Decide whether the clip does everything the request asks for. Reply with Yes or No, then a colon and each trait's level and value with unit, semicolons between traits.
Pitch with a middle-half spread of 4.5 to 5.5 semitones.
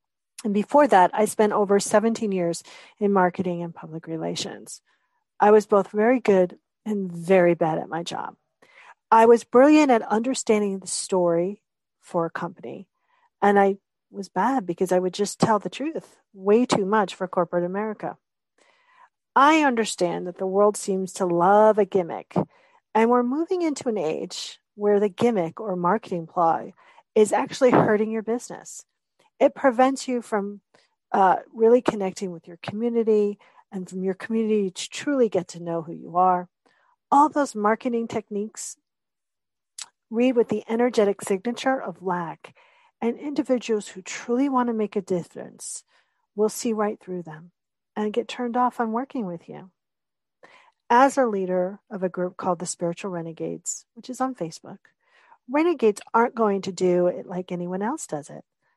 Yes: average, 4.9 semitones